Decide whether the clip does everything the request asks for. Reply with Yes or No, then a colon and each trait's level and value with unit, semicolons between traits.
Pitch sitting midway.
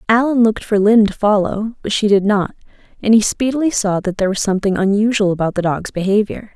No: high, 210 Hz